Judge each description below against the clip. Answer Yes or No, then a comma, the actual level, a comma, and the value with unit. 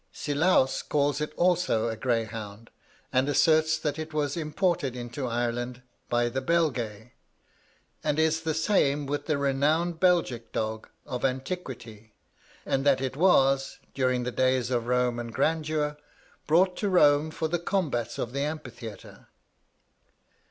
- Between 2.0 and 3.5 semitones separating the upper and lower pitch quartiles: No, average, 4.5 semitones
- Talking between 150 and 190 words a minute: No, average, 140 wpm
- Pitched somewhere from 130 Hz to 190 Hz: Yes, medium, 140 Hz